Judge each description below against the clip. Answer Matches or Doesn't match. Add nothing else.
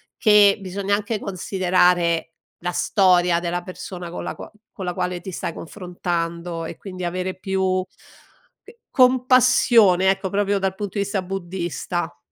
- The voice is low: Doesn't match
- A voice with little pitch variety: Matches